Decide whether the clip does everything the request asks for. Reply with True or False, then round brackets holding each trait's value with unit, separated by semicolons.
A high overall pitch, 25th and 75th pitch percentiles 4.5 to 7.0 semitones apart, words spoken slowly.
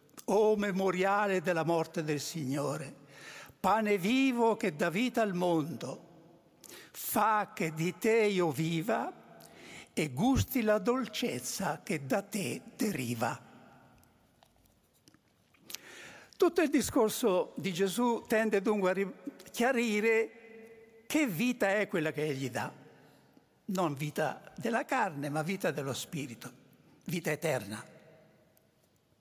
True (200 Hz; 5.1 semitones; 110 wpm)